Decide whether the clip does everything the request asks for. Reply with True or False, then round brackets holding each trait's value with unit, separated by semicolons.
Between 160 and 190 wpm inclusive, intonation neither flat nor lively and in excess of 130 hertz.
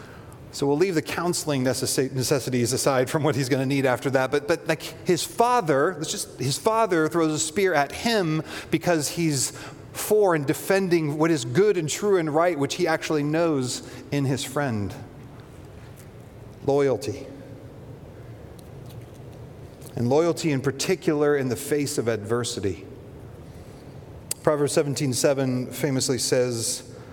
False (135 wpm; 3.7 semitones; 140 Hz)